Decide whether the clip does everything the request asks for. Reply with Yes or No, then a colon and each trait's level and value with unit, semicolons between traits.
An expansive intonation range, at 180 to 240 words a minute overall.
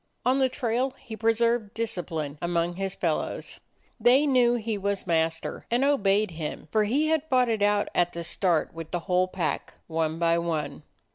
Yes: wide, 5.9 semitones; average, 185 wpm